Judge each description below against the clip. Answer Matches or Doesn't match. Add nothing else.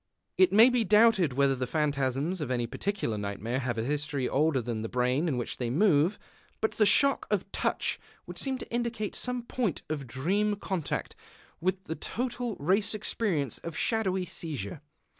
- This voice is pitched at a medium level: Matches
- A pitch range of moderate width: Doesn't match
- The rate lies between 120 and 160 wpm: Doesn't match